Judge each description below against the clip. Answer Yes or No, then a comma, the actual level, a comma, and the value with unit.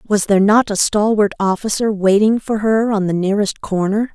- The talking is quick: No, average, 190 wpm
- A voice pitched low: No, high, 205 Hz